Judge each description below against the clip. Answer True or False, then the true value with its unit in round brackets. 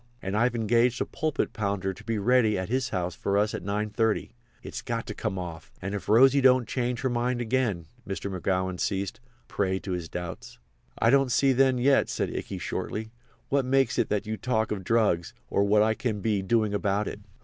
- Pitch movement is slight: False (4.0 semitones)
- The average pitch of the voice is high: False (110 Hz)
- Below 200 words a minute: False (205 wpm)